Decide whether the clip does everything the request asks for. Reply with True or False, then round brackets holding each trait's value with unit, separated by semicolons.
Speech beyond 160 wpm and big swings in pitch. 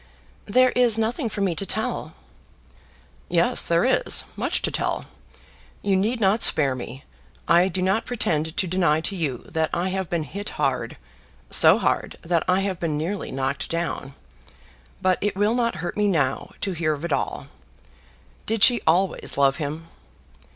False (170 wpm; 4.3 semitones)